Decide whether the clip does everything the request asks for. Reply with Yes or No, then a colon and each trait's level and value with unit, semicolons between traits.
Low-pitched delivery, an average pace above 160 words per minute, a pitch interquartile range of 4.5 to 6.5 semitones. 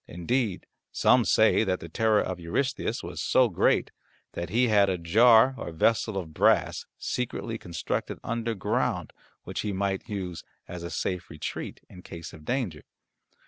No: very low, 95 Hz; average, 155 wpm; average, 4.8 semitones